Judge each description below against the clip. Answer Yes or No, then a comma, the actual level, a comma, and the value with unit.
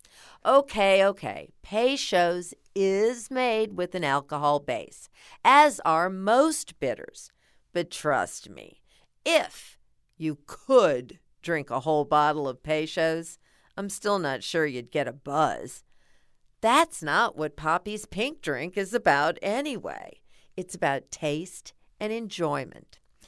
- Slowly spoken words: Yes, slow, 120 wpm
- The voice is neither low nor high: Yes, medium, 175 Hz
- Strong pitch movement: Yes, wide, 5.9 semitones